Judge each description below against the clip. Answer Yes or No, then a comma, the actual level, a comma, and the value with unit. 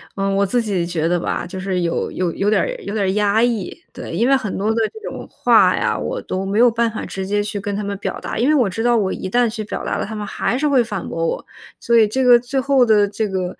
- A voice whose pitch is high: Yes, high, 210 Hz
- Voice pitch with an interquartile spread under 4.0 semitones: Yes, average, 3.6 semitones